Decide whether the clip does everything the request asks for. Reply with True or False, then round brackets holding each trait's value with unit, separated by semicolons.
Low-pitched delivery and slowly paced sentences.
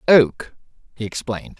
True (120 Hz; 115 wpm)